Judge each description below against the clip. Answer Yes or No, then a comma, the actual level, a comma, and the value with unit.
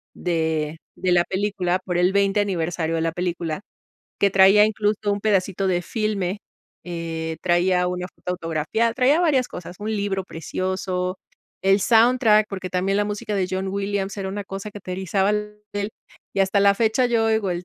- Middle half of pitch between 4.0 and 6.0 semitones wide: No, narrow, 2.5 semitones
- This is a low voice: No, high, 195 Hz